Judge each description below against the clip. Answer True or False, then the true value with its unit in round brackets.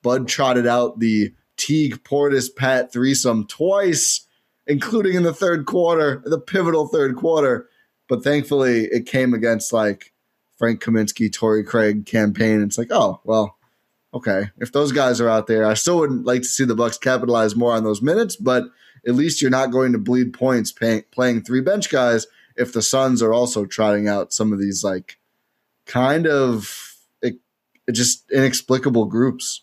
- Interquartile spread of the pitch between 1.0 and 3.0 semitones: False (3.4 semitones)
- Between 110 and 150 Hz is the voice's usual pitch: True (125 Hz)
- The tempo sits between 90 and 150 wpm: False (175 wpm)